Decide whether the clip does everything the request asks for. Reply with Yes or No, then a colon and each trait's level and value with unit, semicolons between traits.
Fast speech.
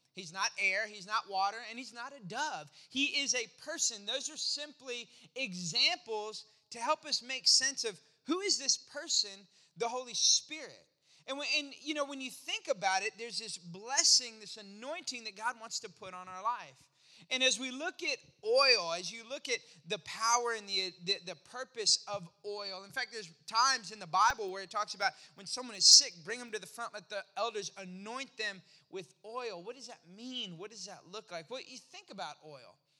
Yes: fast, 210 wpm